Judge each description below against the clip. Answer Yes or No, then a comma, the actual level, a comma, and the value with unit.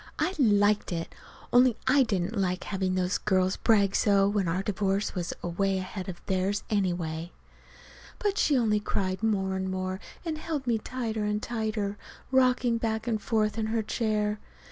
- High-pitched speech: Yes, high, 205 Hz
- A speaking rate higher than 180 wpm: No, average, 170 wpm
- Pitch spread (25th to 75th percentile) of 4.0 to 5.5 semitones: No, average, 3.0 semitones